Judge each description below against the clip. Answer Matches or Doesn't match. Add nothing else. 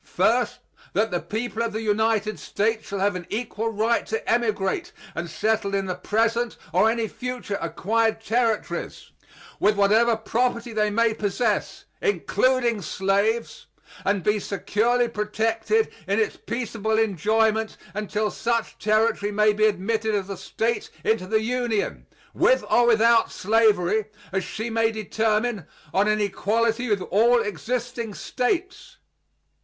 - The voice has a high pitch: Matches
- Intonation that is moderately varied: Doesn't match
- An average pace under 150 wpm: Matches